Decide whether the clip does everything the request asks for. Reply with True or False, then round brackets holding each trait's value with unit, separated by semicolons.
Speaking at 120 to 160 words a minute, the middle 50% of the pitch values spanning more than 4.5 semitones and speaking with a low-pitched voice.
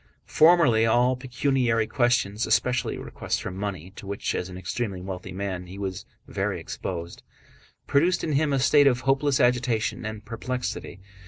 True (155 wpm; 5.2 semitones; 115 Hz)